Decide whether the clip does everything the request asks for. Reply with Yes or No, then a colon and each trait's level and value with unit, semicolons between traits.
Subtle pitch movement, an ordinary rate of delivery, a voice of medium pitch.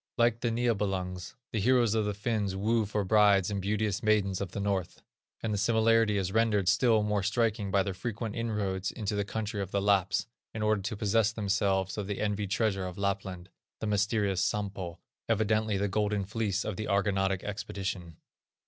No: narrow, 1.9 semitones; average, 185 wpm; low, 105 Hz